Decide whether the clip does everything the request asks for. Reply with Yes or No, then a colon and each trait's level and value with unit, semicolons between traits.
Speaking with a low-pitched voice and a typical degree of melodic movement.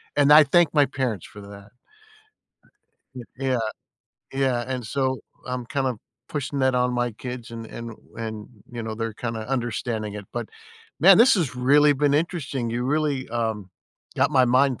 Yes: low, 125 Hz; average, 3.2 semitones